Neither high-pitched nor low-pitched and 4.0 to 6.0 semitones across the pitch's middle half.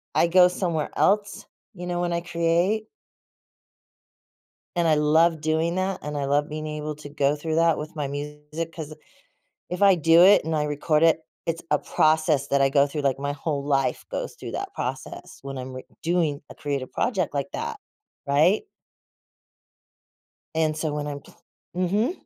No: medium, 155 Hz; average, 2.8 semitones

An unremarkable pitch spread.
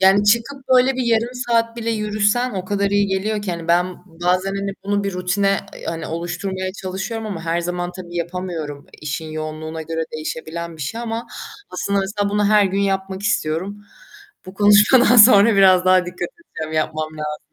Yes: average, 3.5 semitones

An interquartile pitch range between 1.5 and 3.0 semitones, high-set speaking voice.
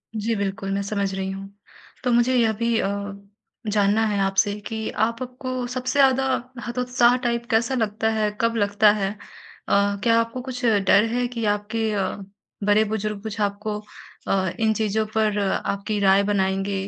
Yes: narrow, 2.6 semitones; high, 215 Hz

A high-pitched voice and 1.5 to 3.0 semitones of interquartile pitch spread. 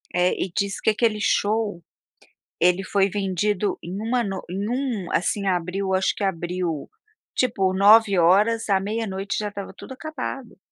Yes: high, 200 Hz; average, 2.7 semitones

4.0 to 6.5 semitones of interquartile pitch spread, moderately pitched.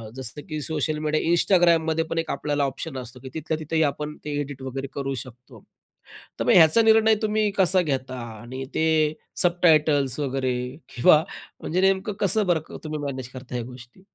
Yes: average, 4.3 semitones; medium, 150 Hz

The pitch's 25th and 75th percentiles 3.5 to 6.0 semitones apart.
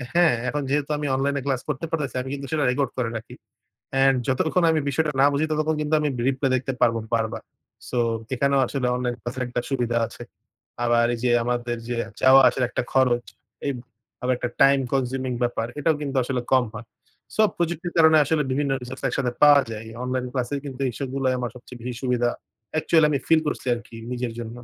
No: average, 2.8 semitones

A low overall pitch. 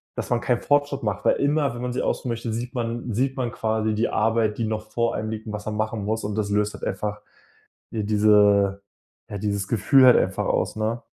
Yes: low, 110 Hz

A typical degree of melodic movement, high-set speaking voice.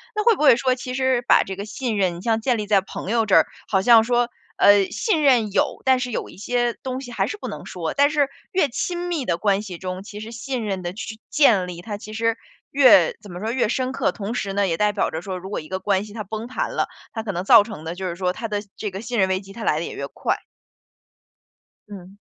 Yes: average, 4.4 semitones; high, 215 Hz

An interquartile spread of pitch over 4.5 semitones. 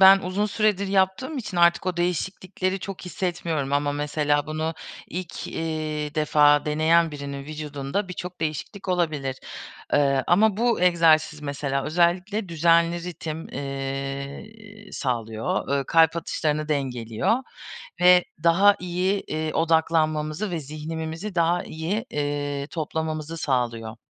No: average, 3.7 semitones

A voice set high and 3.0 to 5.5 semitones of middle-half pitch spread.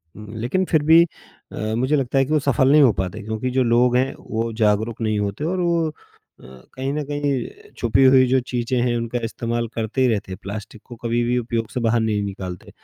No: low, 120 Hz; average, 3.4 semitones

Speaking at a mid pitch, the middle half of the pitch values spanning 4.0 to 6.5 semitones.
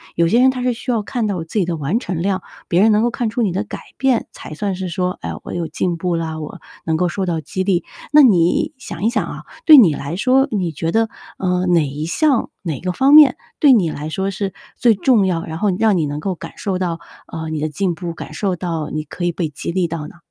Yes: medium, 180 Hz; average, 4.9 semitones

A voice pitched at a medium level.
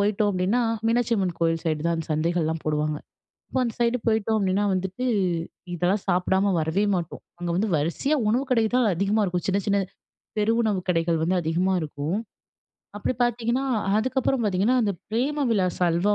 No: high, 195 Hz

